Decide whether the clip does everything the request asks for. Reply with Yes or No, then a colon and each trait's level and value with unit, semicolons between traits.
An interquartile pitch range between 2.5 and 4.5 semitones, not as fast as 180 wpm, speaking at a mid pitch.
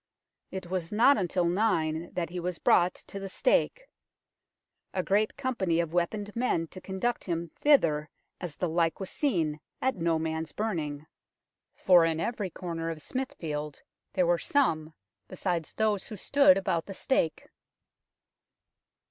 Yes: average, 4.2 semitones; average, 150 wpm; medium, 180 Hz